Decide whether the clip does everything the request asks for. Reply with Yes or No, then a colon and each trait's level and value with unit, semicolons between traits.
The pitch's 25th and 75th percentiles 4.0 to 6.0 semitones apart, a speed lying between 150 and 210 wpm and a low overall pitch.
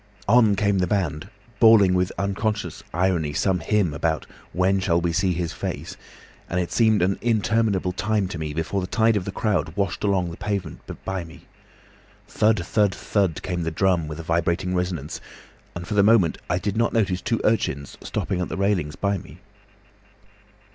No: average, 3.2 semitones; average, 180 wpm; very low, 95 Hz